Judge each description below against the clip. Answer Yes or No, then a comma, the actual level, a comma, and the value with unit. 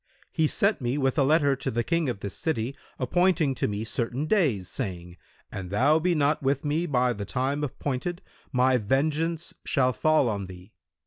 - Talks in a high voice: No, low, 135 Hz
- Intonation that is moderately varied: Yes, average, 5.0 semitones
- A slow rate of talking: No, average, 185 wpm